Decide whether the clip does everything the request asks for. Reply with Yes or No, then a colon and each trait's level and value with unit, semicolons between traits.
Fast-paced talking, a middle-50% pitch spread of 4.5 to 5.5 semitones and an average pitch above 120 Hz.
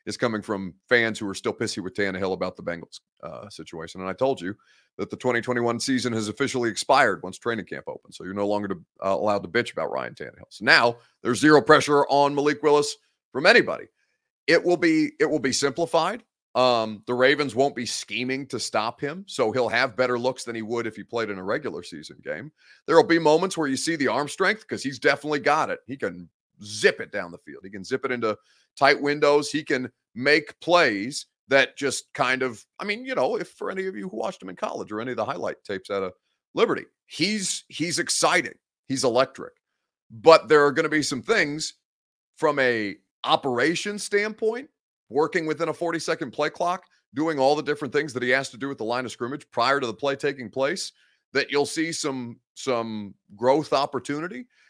Yes: fast, 210 wpm; average, 4.8 semitones; low, 135 Hz